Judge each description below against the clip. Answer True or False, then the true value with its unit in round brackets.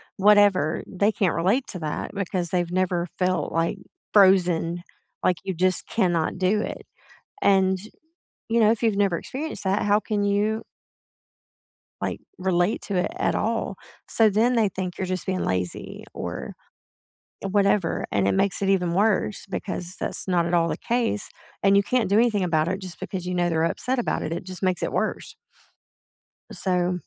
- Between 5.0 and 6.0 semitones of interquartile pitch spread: False (2.6 semitones)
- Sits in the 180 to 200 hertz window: True (190 Hz)